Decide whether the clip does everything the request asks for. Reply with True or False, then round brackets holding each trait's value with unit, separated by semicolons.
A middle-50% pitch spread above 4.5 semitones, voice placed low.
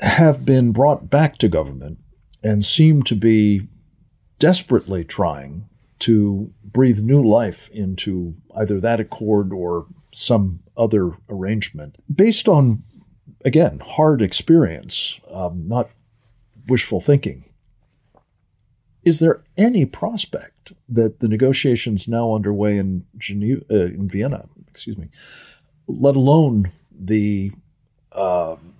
True (5.0 semitones; 110 Hz)